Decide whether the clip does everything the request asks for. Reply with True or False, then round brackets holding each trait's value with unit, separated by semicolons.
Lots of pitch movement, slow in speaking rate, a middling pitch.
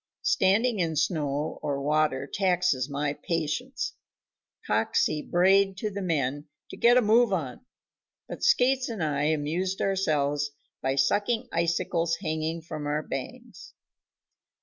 False (4.8 semitones; 125 wpm; 165 Hz)